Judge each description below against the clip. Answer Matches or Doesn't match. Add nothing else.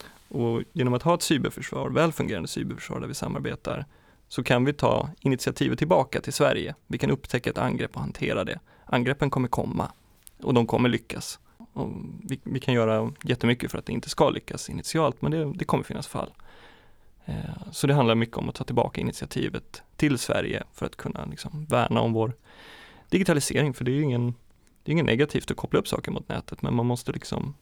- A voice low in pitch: Matches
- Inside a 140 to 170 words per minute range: Doesn't match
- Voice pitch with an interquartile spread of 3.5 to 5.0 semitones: Matches